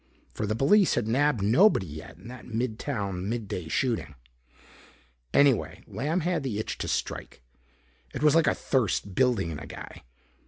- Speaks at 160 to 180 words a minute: Yes, average, 170 wpm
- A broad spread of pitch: Yes, wide, 6.0 semitones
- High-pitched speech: No, low, 115 Hz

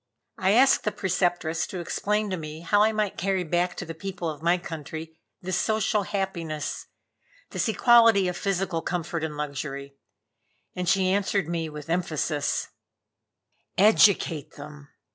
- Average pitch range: Yes, average, 3.6 semitones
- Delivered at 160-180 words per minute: No, average, 145 wpm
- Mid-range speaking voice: Yes, medium, 175 Hz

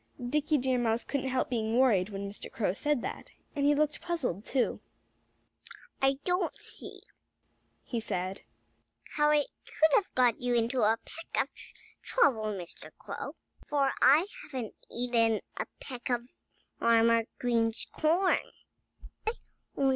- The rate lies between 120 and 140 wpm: Yes, slow, 135 wpm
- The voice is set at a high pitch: Yes, high, 245 Hz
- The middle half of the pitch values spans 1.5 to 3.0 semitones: No, average, 4.4 semitones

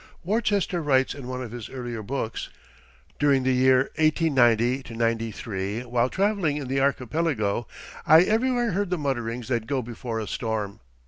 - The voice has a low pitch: Yes, low, 130 Hz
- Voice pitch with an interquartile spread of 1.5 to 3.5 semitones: No, average, 5.0 semitones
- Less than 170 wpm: Yes, average, 150 wpm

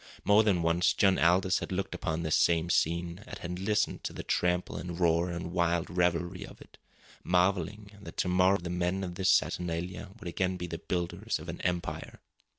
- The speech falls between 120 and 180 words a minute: No, average, 195 wpm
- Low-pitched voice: Yes, very low, 90 Hz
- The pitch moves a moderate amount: No, narrow, 1.5 semitones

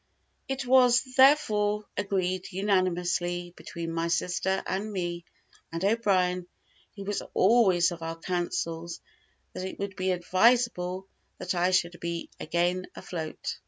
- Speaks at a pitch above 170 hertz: Yes, medium, 185 Hz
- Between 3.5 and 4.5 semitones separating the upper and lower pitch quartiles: No, average, 2.7 semitones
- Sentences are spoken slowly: Yes, slow, 125 wpm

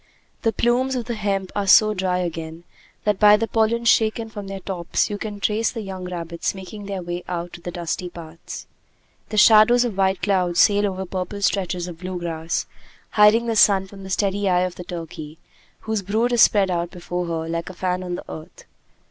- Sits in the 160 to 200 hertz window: Yes, high, 190 Hz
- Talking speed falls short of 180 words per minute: No, fast, 205 wpm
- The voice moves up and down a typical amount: Yes, average, 3.1 semitones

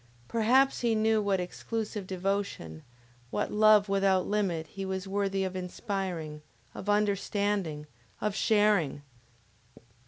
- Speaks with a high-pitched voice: Yes, high, 200 Hz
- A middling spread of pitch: No, narrow, 2.3 semitones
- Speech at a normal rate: No, slow, 115 wpm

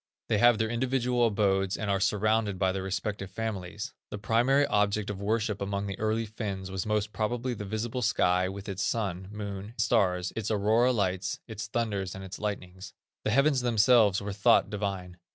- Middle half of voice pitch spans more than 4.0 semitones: No, narrow, 2.6 semitones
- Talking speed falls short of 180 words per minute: No, average, 185 wpm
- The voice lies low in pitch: Yes, low, 105 Hz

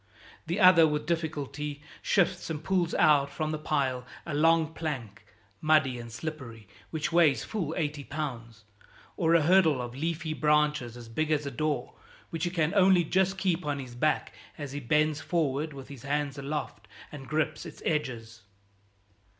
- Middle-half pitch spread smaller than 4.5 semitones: Yes, average, 2.9 semitones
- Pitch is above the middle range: No, medium, 150 Hz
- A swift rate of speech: No, average, 165 wpm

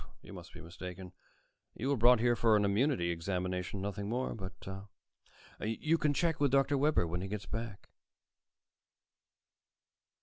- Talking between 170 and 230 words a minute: No, average, 145 wpm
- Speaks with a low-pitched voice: Yes, low, 105 Hz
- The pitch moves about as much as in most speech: No, wide, 5.9 semitones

